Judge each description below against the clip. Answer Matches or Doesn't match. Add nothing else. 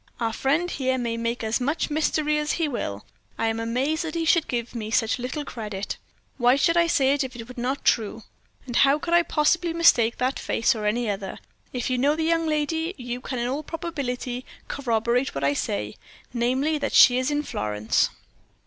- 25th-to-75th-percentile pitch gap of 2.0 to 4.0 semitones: Doesn't match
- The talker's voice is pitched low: Doesn't match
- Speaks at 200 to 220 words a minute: Matches